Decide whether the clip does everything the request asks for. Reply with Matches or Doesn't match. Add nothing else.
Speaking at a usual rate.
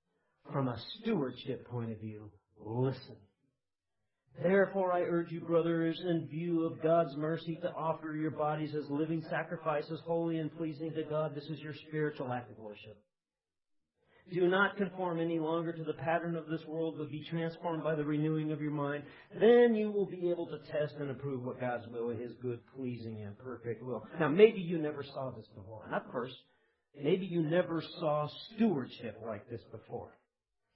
Matches